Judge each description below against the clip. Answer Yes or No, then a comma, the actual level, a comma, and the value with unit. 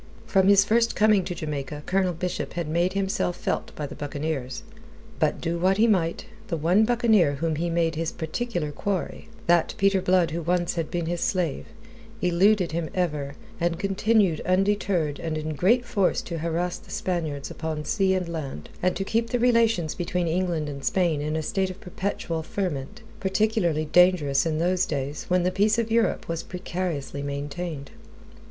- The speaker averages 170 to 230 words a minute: Yes, average, 175 wpm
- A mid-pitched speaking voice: Yes, medium, 175 Hz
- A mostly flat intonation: No, average, 3.6 semitones